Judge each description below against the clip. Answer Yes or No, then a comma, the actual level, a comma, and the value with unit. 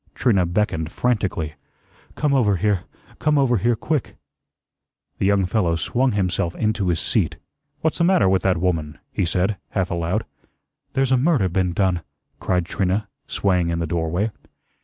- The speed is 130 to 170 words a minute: Yes, average, 160 wpm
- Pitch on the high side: No, very low, 95 Hz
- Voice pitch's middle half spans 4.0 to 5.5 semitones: Yes, average, 4.5 semitones